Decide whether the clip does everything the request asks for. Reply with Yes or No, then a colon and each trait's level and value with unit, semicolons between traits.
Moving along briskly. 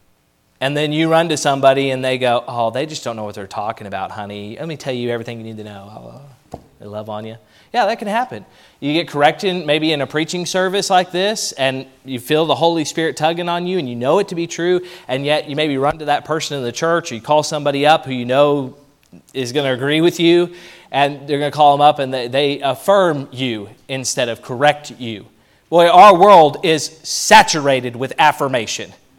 Yes: fast, 225 wpm